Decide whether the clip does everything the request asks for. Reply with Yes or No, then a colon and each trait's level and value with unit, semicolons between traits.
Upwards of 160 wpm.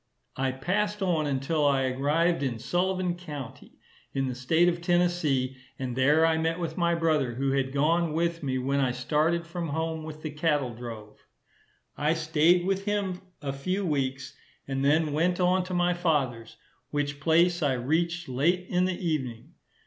Yes: average, 170 wpm